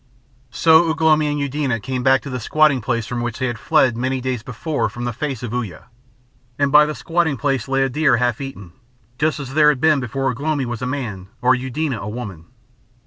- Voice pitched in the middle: No, low, 130 Hz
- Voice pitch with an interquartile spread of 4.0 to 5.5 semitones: No, average, 3.5 semitones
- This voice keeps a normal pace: No, fast, 215 wpm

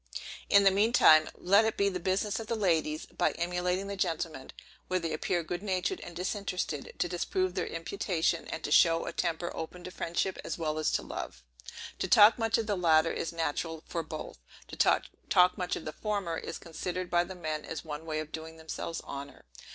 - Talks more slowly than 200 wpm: No, fast, 205 wpm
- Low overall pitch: No, medium, 175 Hz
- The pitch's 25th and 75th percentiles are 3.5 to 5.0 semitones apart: No, average, 2.8 semitones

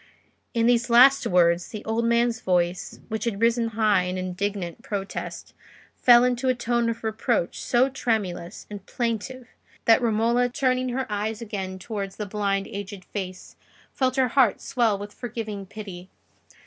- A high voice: Yes, high, 220 Hz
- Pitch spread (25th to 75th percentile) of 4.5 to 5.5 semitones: No, average, 3.4 semitones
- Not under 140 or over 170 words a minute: Yes, average, 155 wpm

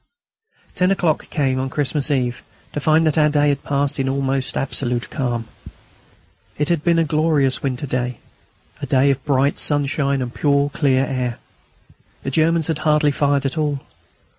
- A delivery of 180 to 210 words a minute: No, average, 165 wpm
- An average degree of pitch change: No, narrow, 2.3 semitones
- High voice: No, medium, 140 Hz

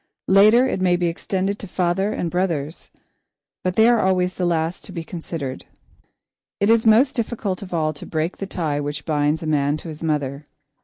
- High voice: No, medium, 175 Hz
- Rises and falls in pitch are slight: No, average, 4.0 semitones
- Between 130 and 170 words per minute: No, average, 195 wpm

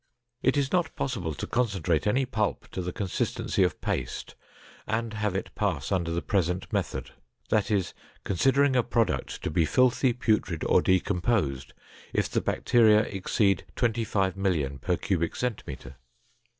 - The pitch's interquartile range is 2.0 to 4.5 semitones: No, average, 4.9 semitones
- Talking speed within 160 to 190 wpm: No, average, 145 wpm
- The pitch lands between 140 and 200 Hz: No, low, 100 Hz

